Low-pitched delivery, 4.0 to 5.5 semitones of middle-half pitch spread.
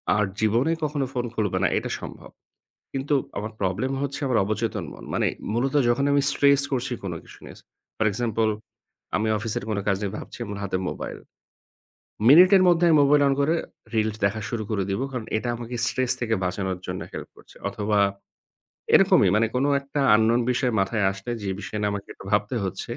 Yes: low, 115 Hz; average, 4.4 semitones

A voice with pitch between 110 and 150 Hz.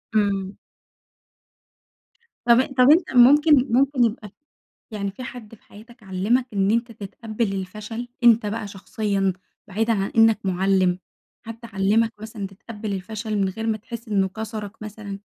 No: high, 215 Hz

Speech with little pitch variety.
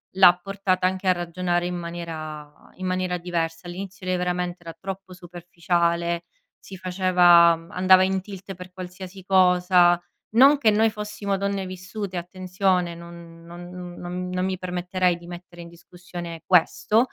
Yes: narrow, 1.3 semitones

